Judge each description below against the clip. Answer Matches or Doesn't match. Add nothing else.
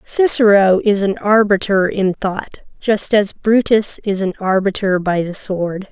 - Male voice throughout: Doesn't match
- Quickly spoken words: Doesn't match